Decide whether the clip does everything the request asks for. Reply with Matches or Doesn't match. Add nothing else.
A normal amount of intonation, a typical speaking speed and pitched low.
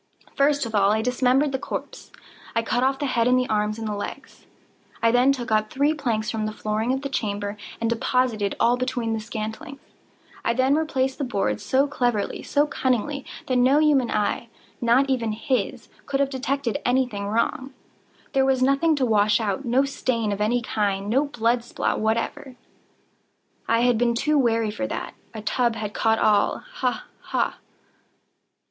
Doesn't match